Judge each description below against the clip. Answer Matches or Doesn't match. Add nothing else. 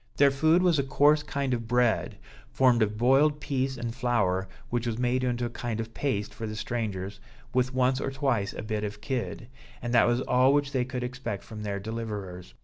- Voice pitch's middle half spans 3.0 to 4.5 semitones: Matches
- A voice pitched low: Matches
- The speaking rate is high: Matches